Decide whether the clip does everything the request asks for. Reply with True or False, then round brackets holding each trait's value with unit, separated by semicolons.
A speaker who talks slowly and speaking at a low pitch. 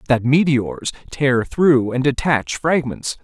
True (130 wpm; 130 Hz)